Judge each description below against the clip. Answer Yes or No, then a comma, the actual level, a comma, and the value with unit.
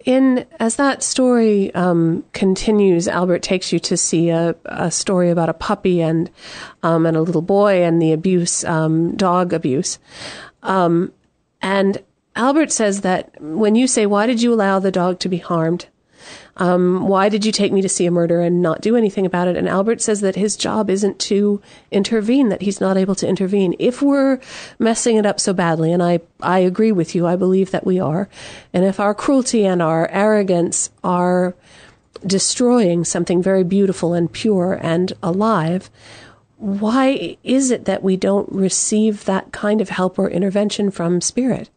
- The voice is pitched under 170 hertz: No, high, 190 Hz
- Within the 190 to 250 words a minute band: No, average, 180 wpm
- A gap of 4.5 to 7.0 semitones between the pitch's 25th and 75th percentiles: No, average, 3.2 semitones